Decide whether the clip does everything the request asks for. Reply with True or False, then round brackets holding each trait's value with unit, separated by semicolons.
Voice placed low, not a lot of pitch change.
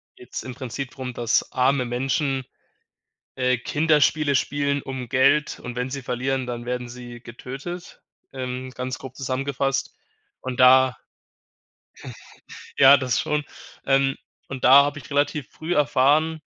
True (130 Hz; 2.0 semitones)